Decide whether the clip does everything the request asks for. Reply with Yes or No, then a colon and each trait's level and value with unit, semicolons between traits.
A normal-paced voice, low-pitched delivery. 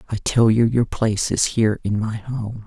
No: fast, 225 wpm; low, 110 Hz